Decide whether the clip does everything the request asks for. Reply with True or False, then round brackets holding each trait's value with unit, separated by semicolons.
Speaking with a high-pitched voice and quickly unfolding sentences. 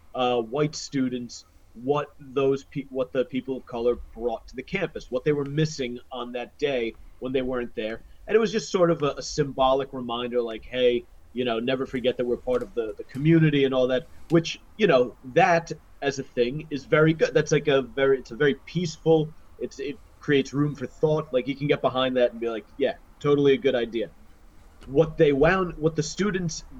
False (135 Hz; 215 wpm)